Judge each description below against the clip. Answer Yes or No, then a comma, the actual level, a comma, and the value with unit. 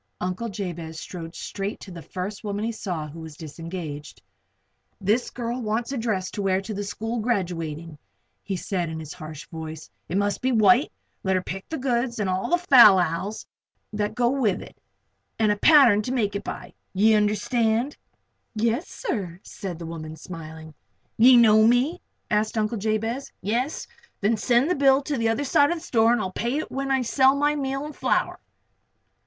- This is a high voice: Yes, high, 215 Hz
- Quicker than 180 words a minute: Yes, average, 190 wpm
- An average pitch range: Yes, average, 5.0 semitones